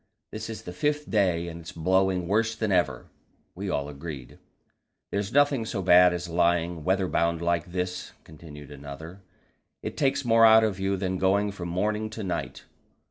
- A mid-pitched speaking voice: No, very low, 90 Hz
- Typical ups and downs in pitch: Yes, average, 3.9 semitones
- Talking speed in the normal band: Yes, average, 175 wpm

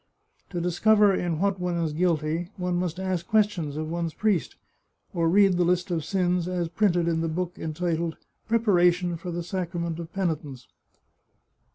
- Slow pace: No, average, 170 wpm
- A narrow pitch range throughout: Yes, narrow, 1.8 semitones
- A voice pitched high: No, medium, 175 Hz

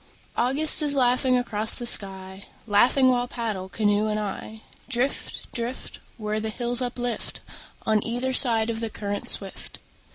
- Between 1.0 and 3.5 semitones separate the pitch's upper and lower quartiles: Yes, average, 2.8 semitones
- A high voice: Yes, high, 230 Hz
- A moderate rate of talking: Yes, average, 150 wpm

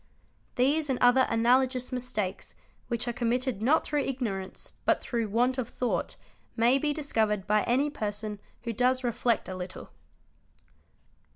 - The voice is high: Yes, high, 245 Hz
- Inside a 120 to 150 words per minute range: Yes, average, 145 wpm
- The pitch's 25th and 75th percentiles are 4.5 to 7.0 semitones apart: No, average, 3.0 semitones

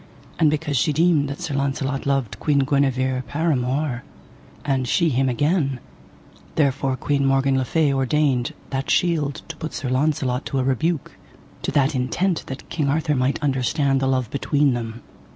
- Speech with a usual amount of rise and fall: No, narrow, 2.3 semitones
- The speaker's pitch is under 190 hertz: Yes, medium, 140 Hz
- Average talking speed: Yes, average, 165 wpm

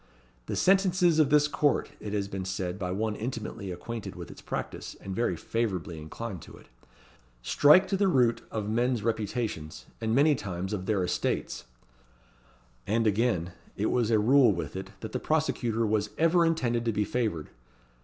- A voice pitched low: Yes, low, 110 Hz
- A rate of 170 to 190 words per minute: Yes, average, 175 wpm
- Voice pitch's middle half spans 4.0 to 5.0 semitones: Yes, average, 4.7 semitones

